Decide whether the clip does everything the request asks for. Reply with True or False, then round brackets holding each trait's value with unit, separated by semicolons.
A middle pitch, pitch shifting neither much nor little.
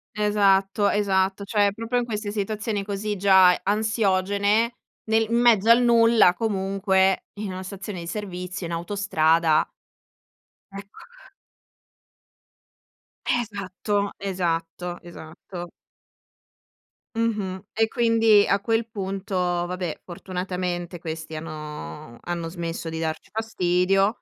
False (195 Hz; 3.1 semitones)